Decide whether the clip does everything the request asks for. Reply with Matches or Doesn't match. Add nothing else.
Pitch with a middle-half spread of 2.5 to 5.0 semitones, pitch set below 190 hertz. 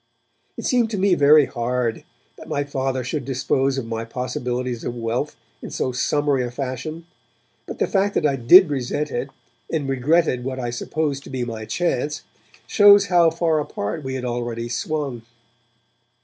Matches